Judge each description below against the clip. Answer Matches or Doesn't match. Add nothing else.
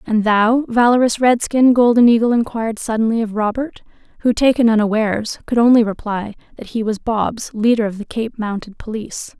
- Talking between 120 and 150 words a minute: Doesn't match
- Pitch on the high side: Matches